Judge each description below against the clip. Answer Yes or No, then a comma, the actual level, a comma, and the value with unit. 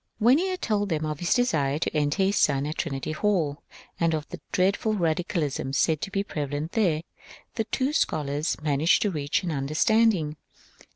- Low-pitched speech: No, medium, 160 Hz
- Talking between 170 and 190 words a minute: Yes, average, 180 wpm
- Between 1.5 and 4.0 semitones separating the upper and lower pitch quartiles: No, wide, 5.5 semitones